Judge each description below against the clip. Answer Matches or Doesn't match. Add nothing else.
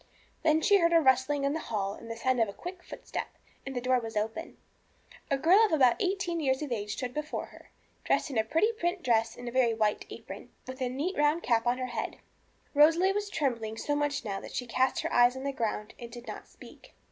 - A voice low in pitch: Doesn't match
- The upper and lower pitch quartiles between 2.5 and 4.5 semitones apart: Doesn't match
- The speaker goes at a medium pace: Doesn't match